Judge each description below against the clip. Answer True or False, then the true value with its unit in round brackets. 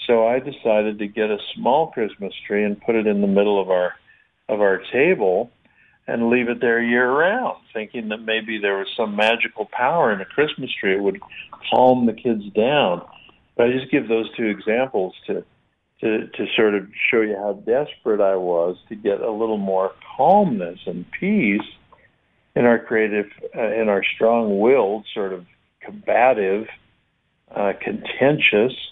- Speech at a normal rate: True (170 wpm)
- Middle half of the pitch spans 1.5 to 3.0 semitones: True (2.6 semitones)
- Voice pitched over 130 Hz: False (110 Hz)